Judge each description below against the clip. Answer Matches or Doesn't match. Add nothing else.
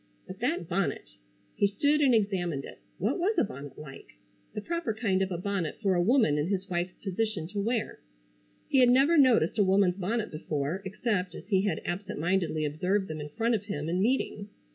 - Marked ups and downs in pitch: Doesn't match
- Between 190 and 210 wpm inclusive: Matches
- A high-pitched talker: Matches